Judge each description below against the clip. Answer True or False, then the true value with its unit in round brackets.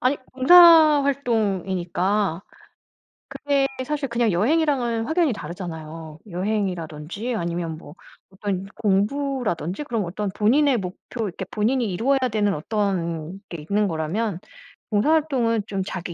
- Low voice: False (205 Hz)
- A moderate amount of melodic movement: False (5.9 semitones)